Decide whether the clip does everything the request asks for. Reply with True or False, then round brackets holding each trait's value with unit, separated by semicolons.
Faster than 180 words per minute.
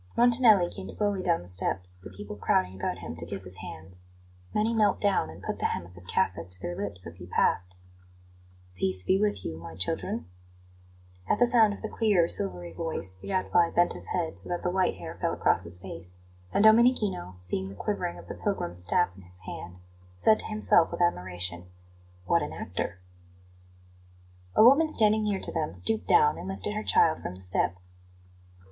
True (195 wpm)